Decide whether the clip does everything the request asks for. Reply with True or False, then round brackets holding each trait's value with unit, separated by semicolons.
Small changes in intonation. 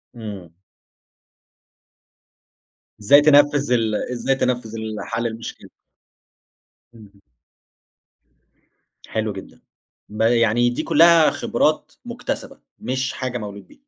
False (3.3 semitones)